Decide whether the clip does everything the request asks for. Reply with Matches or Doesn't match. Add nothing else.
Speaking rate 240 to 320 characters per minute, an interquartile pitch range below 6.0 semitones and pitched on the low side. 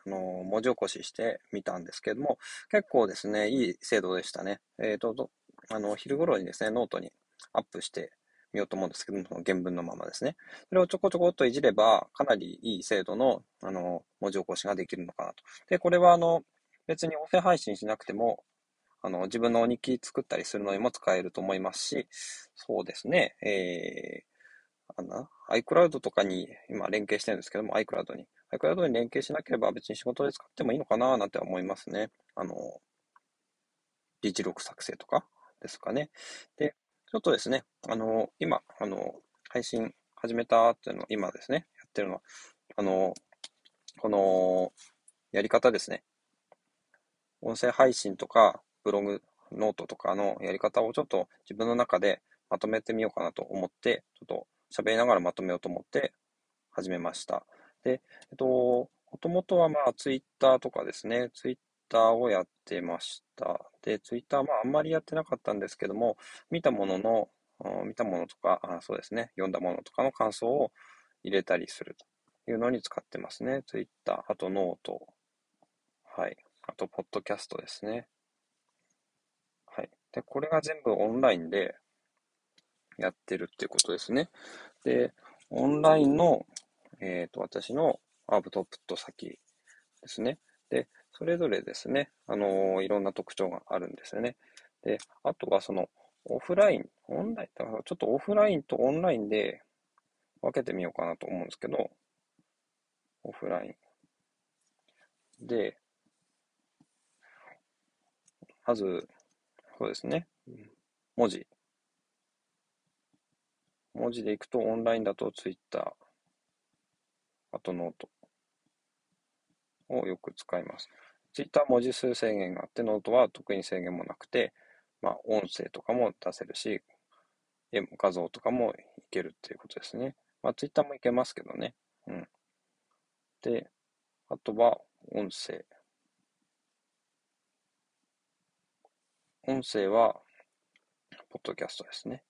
Matches